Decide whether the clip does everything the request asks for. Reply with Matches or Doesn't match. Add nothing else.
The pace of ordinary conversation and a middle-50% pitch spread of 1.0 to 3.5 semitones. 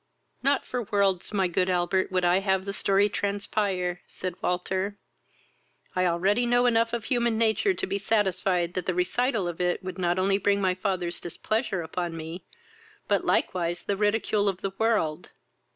Matches